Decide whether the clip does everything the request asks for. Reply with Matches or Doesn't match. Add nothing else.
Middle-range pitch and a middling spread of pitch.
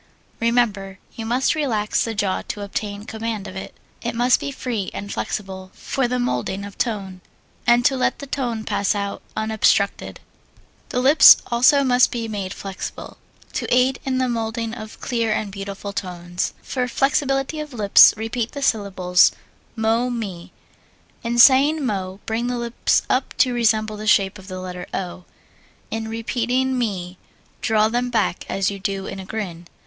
Doesn't match